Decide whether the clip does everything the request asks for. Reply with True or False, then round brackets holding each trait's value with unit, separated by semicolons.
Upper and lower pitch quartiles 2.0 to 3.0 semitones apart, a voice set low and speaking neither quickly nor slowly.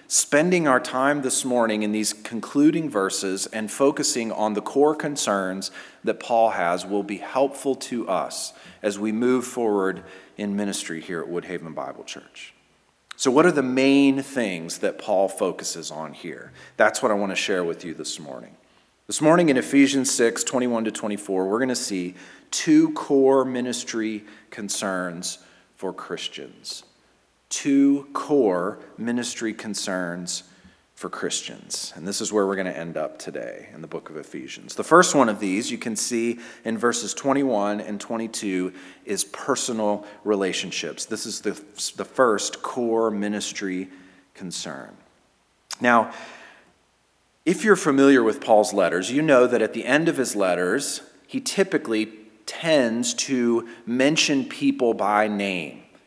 False (4.9 semitones; 110 Hz; 150 wpm)